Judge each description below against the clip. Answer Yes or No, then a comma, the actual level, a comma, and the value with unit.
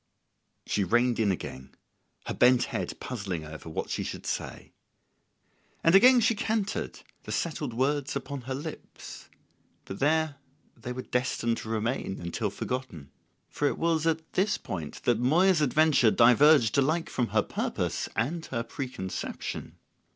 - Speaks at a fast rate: No, average, 145 wpm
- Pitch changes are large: Yes, wide, 5.7 semitones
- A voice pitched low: Yes, low, 130 Hz